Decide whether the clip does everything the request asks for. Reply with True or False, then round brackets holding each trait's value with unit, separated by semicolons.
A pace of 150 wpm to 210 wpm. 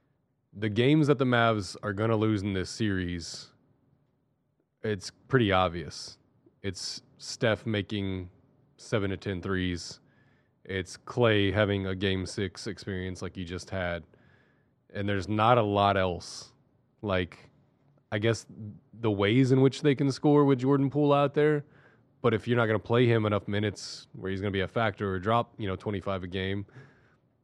True (170 wpm)